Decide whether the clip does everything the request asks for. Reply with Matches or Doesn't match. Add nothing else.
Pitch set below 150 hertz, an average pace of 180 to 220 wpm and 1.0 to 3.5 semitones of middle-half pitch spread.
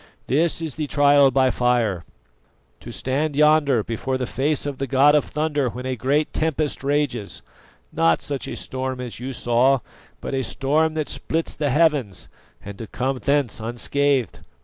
Doesn't match